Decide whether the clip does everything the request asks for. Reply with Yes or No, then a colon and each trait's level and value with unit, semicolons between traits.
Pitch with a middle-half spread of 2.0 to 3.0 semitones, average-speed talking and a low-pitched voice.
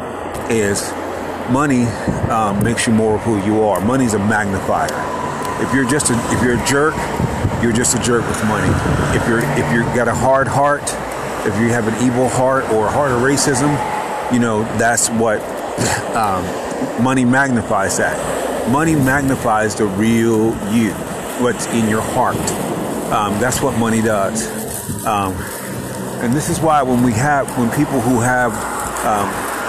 Yes: average, 2.7 semitones; average, 165 wpm; low, 120 Hz